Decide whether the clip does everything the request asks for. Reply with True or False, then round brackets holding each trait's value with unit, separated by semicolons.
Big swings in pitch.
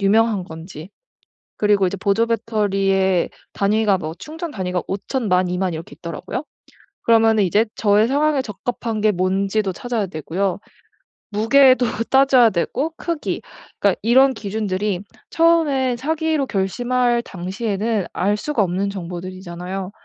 False (4.4 semitones)